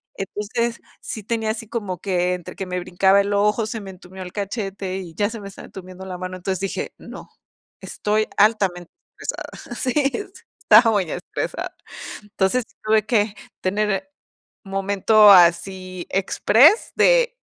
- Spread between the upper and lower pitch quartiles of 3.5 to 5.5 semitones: No, average, 2.7 semitones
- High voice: Yes, high, 200 Hz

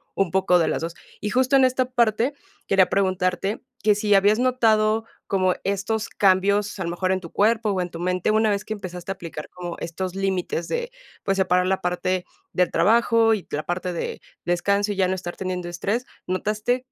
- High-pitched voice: Yes, high, 195 Hz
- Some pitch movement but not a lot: Yes, average, 3.0 semitones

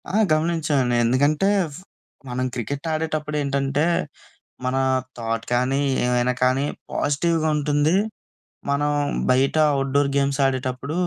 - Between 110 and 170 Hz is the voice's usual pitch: Yes, medium, 140 Hz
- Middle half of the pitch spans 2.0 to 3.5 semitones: Yes, average, 2.8 semitones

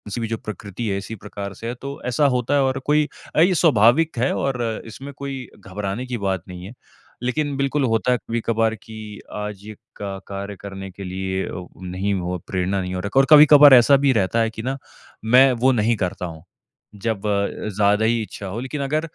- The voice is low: Yes, low, 110 Hz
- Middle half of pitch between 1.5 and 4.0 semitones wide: No, average, 5.0 semitones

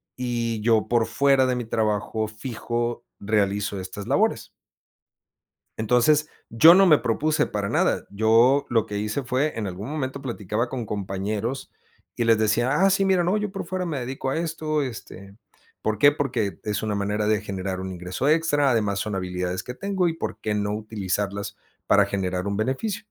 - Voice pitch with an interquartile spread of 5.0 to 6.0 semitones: Yes, average, 5.3 semitones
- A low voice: Yes, low, 115 Hz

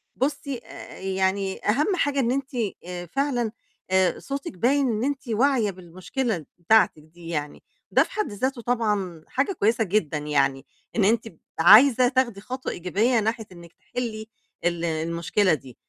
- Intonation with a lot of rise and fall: Yes, wide, 6.6 semitones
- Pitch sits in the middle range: No, high, 215 Hz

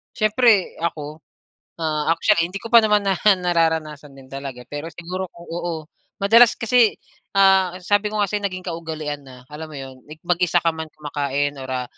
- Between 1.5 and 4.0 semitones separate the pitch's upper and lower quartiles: No, average, 4.8 semitones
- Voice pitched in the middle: Yes, medium, 165 Hz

